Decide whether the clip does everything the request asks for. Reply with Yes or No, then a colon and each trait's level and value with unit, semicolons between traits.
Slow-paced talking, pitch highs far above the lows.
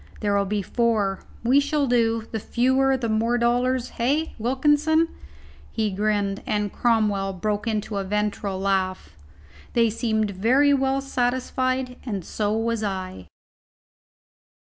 No: slow, 125 wpm; average, 3.9 semitones